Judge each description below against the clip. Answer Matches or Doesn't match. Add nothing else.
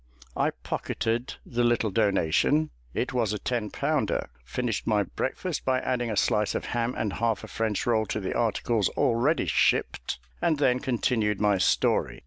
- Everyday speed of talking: Matches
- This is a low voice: Matches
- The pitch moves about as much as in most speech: Matches